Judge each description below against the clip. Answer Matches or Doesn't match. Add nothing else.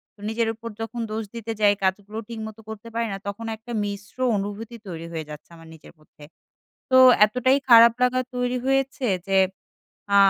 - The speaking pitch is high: Matches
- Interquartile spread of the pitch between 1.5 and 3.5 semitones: Matches